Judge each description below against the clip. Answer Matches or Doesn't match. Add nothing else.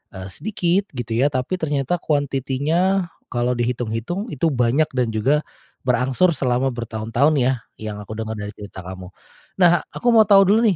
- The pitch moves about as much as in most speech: Doesn't match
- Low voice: Matches